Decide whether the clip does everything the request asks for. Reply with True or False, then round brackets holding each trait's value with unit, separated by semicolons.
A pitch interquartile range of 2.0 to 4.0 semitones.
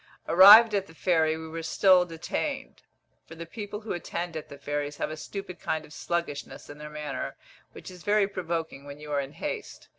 True (3.5 semitones)